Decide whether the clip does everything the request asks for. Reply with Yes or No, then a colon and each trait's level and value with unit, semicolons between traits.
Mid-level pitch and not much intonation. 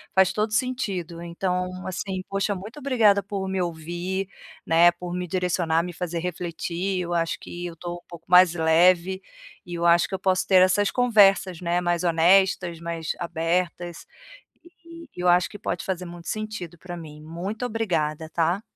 Yes: medium, 180 Hz; narrow, 2.1 semitones